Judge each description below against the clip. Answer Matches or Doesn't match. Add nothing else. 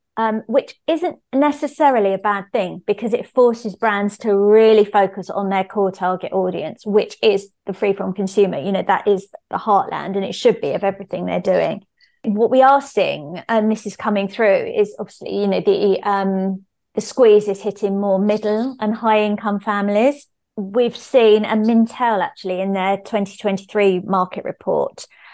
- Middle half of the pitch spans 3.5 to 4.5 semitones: Doesn't match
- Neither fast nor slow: Matches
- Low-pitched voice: Doesn't match